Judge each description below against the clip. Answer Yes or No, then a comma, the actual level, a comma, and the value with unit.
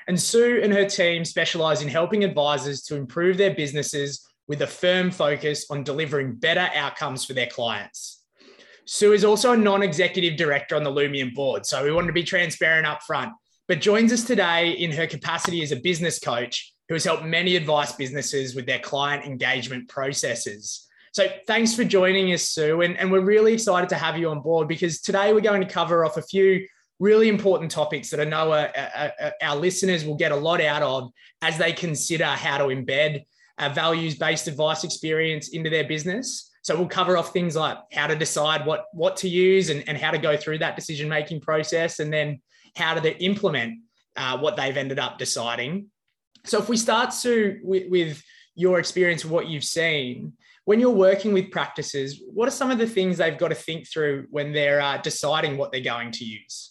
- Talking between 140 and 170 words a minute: No, average, 200 wpm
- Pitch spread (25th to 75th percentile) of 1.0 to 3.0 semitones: No, average, 4.0 semitones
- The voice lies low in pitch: No, medium, 160 Hz